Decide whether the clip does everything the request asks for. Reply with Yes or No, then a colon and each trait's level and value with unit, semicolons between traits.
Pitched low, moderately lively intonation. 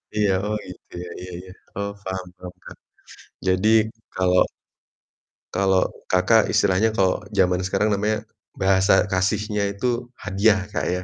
No: very low, 95 Hz; narrow, 2.1 semitones